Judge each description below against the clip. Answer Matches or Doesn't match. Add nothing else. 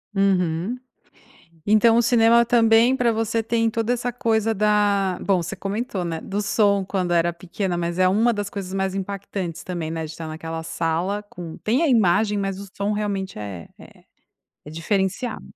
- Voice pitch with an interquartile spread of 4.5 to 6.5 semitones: Doesn't match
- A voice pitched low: Doesn't match